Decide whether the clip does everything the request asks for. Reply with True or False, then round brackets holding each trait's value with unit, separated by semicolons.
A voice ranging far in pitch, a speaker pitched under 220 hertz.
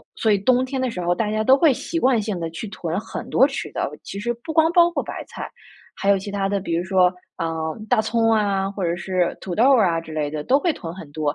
True (5.9 semitones; 200 Hz)